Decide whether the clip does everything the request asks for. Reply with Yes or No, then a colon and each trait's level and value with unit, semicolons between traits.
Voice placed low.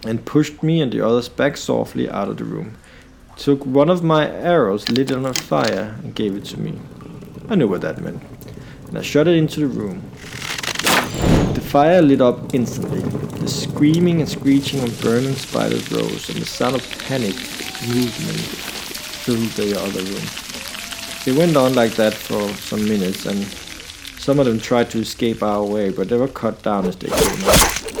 Yes: low, 125 Hz